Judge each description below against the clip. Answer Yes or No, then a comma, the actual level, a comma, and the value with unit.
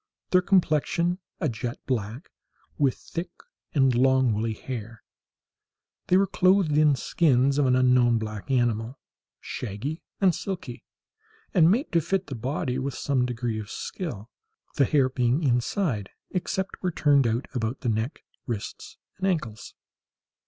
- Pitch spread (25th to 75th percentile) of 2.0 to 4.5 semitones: No, wide, 5.6 semitones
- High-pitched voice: No, low, 130 Hz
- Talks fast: No, average, 145 wpm